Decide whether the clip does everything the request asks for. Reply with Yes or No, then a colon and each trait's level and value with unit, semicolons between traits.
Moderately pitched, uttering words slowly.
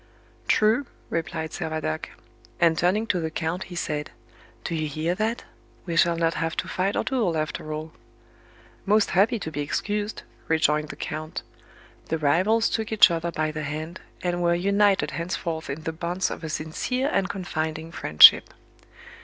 No: medium, 170 Hz; average, 165 wpm